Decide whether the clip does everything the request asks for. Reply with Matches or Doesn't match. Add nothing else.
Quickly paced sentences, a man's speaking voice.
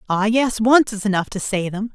Doesn't match